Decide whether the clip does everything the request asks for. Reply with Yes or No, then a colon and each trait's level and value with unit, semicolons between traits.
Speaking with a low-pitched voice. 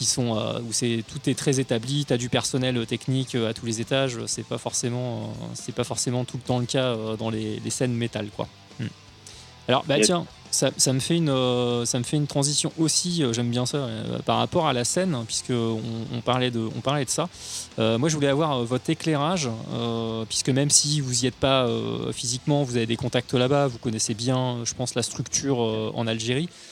Yes: low, 125 Hz